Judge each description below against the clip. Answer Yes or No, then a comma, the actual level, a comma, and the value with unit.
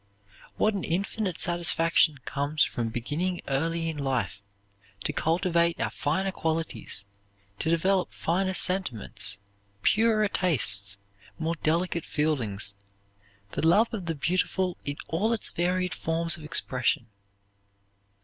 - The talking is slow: Yes, slow, 120 wpm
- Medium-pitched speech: Yes, medium, 165 Hz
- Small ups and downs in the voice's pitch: No, average, 4.2 semitones